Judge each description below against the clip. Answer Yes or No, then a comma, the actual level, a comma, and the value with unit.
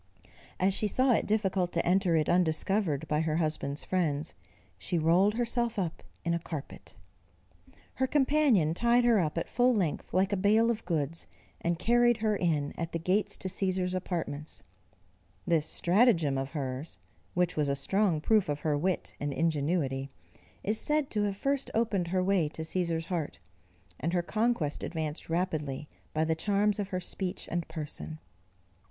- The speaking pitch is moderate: Yes, medium, 175 Hz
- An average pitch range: Yes, average, 4.8 semitones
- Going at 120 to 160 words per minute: No, average, 170 wpm